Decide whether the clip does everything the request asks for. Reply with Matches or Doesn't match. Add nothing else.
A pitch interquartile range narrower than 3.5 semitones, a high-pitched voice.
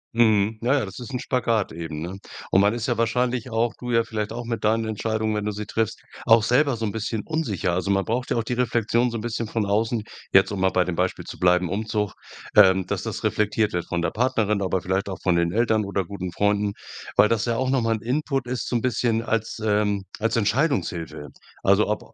Doesn't match